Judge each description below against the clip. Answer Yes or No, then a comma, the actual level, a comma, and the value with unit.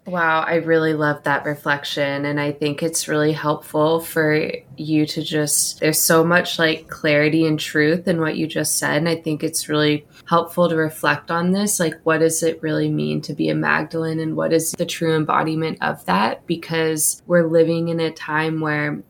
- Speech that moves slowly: No, average, 200 wpm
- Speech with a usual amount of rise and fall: No, narrow, 1.5 semitones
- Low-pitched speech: No, medium, 160 Hz